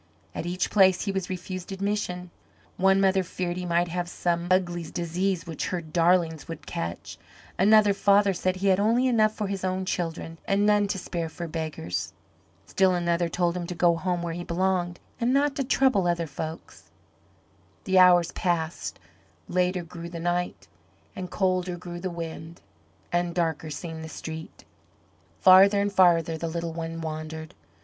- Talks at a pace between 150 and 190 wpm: Yes, average, 170 wpm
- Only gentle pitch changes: Yes, narrow, 2.1 semitones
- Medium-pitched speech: Yes, medium, 175 Hz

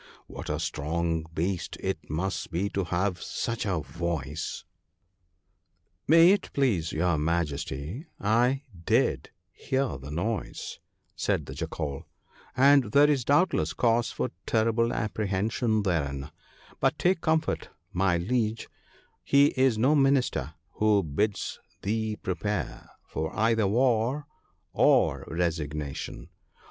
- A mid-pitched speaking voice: No, low, 100 Hz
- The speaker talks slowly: Yes, slow, 125 wpm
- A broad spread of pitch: Yes, wide, 6.2 semitones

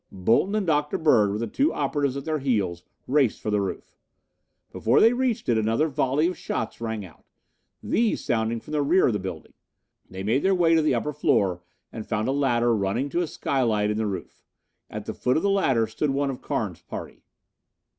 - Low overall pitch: Yes, low, 125 Hz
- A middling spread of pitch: No, wide, 5.9 semitones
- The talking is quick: Yes, fast, 210 wpm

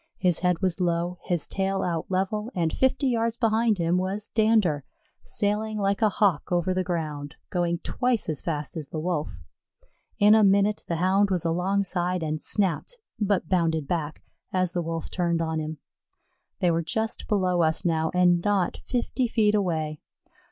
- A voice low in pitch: No, medium, 180 Hz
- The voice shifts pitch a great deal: No, average, 3.8 semitones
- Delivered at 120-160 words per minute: No, average, 170 wpm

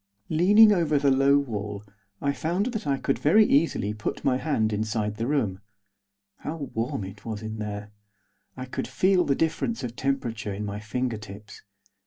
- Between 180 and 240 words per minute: No, average, 170 wpm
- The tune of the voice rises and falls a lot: Yes, wide, 6.0 semitones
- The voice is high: No, low, 125 Hz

